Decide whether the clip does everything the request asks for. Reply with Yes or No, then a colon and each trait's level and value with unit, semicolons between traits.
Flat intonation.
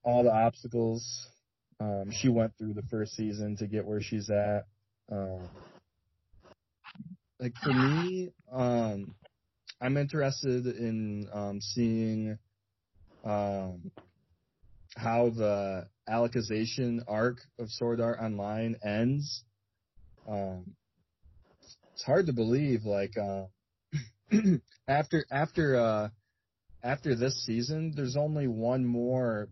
No: average, 3.4 semitones